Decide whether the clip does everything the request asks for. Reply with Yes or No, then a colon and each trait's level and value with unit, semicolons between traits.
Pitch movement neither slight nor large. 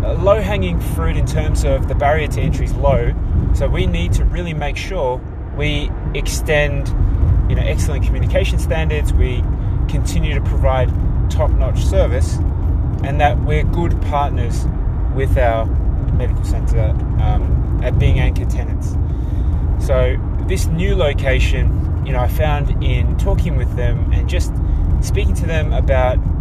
Yes: average, 3.7 semitones